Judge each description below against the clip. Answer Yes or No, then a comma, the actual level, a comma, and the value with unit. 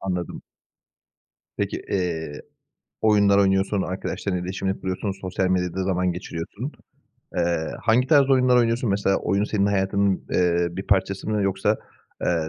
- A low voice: Yes, very low, 95 Hz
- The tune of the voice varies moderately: No, narrow, 2.1 semitones